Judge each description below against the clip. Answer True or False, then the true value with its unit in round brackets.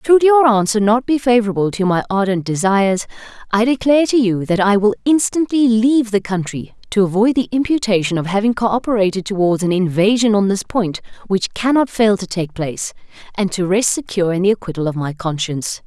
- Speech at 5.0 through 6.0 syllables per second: True (5.7 syllables/s)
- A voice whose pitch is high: True (210 Hz)